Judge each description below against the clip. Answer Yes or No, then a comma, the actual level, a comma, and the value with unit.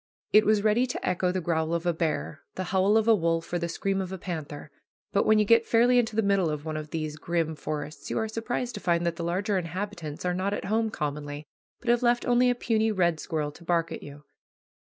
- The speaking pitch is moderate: Yes, medium, 180 Hz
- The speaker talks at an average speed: No, fast, 245 wpm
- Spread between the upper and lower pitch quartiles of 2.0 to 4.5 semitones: No, average, 5.1 semitones